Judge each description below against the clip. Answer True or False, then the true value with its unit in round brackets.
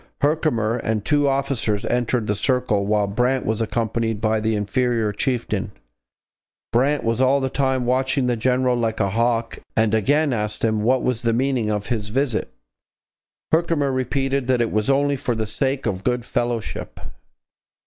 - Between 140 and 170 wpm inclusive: True (165 wpm)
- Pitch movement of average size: True (3.2 semitones)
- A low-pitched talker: True (120 Hz)